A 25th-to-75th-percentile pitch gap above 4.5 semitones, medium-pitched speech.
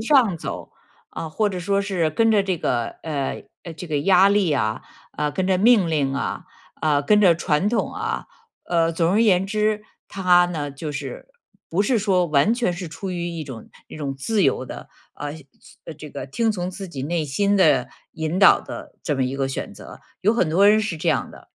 Yes: average, 5.1 semitones; medium, 175 Hz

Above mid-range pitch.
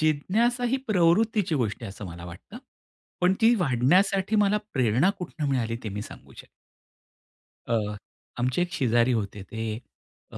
No: medium, 145 Hz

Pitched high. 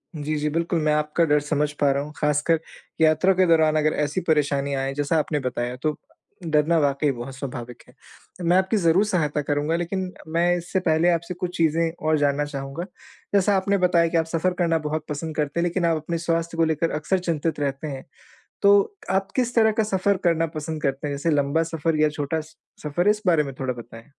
No: medium, 155 Hz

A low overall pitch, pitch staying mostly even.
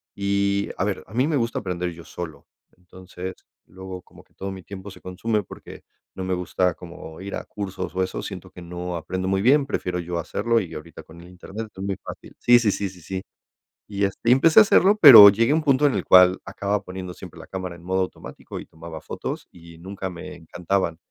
Yes: very low, 95 Hz; narrow, 2.2 semitones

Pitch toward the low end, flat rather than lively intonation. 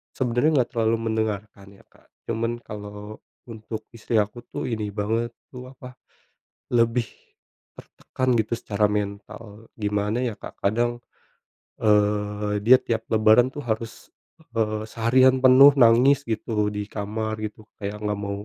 Yes: low, 110 Hz; narrow, 2.3 semitones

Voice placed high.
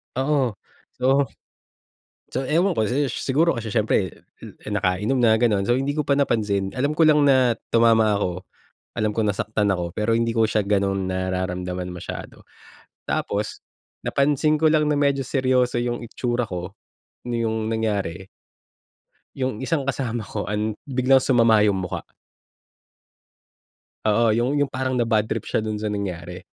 No: low, 115 Hz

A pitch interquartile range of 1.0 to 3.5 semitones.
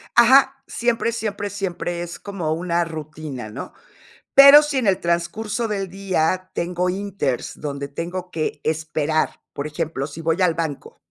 No: average, 4.4 semitones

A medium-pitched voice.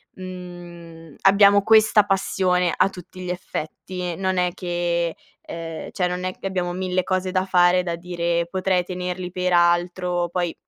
Yes: medium, 180 Hz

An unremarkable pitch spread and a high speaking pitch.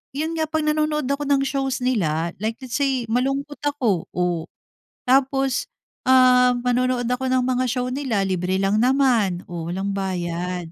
No: wide, 6.0 semitones; very high, 250 Hz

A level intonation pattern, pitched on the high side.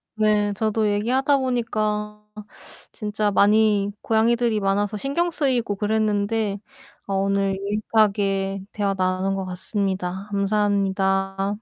Yes: narrow, 1.8 semitones; high, 205 Hz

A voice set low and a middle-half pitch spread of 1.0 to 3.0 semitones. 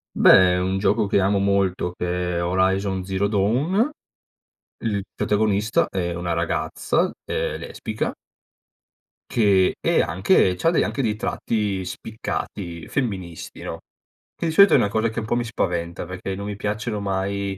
Yes: low, 100 Hz; average, 2.7 semitones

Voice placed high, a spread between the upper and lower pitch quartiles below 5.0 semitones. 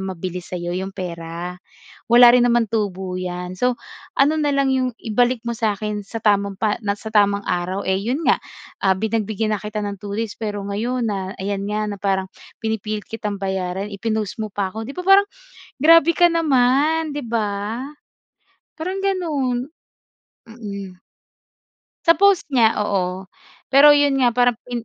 Yes: high, 215 Hz; average, 4.6 semitones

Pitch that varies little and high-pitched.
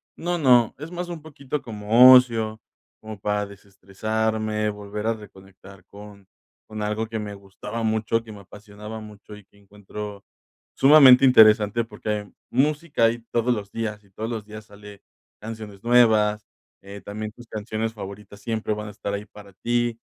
No: narrow, 1.9 semitones; low, 110 Hz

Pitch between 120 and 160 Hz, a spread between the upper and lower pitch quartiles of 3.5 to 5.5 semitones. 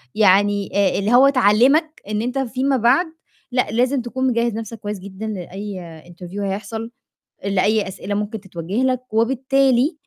No: high, 220 Hz; average, 4.1 semitones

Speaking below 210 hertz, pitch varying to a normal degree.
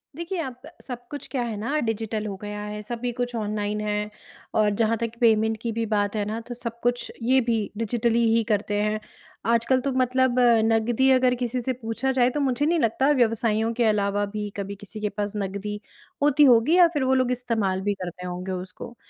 No: high, 230 Hz; average, 3.1 semitones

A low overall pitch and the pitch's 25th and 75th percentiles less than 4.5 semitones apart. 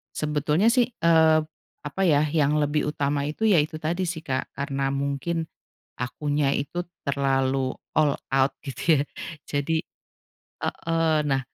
No: medium, 150 Hz; narrow, 2.6 semitones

